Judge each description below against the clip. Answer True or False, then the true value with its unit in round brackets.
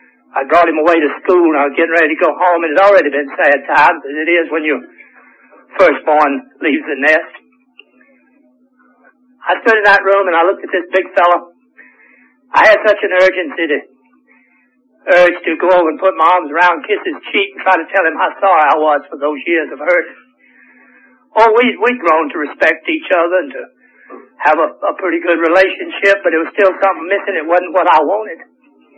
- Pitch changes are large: True (7.0 semitones)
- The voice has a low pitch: False (185 Hz)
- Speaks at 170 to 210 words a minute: True (205 wpm)